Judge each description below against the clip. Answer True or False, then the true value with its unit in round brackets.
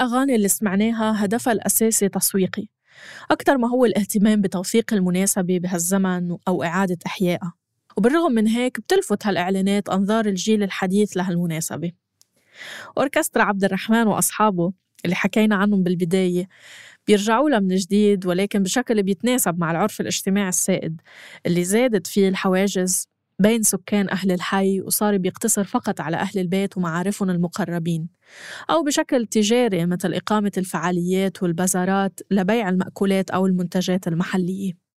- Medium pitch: False (195 Hz)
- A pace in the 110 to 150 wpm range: True (125 wpm)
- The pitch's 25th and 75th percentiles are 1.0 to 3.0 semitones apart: True (2.7 semitones)